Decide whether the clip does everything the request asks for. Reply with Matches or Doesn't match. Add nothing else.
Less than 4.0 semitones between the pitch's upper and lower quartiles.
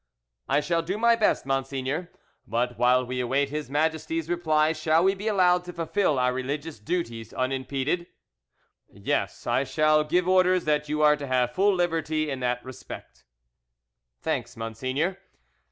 Doesn't match